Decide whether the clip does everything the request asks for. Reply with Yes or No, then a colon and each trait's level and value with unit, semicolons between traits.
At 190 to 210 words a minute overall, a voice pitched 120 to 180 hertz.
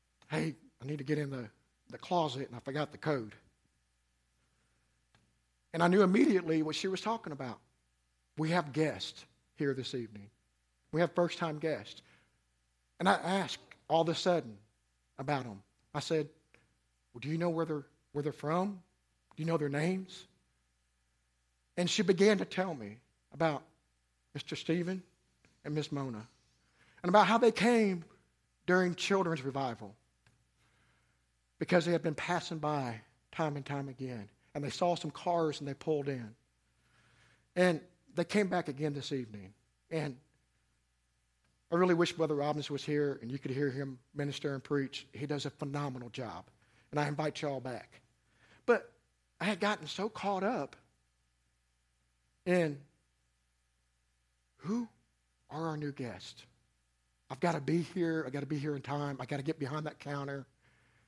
No: average, 160 wpm; medium, 140 Hz